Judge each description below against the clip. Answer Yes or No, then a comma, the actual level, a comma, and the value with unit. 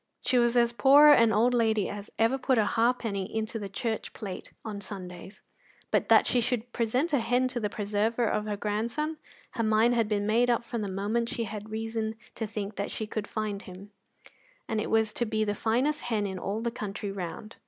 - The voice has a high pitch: Yes, high, 220 Hz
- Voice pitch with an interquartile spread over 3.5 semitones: No, narrow, 2.4 semitones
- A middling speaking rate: No, fast, 210 wpm